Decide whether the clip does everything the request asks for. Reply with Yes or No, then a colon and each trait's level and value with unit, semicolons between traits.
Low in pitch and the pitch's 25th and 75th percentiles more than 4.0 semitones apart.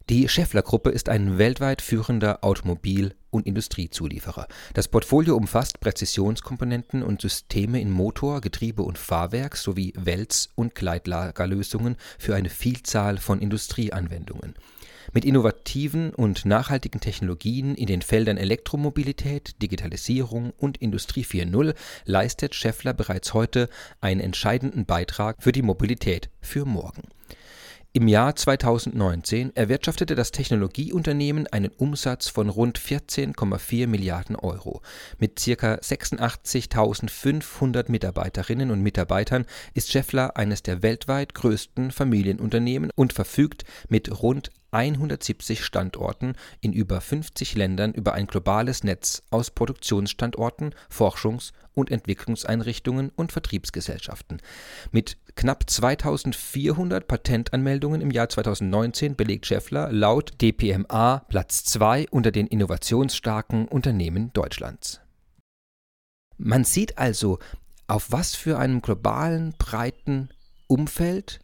Yes: low, 115 Hz; average, 4.7 semitones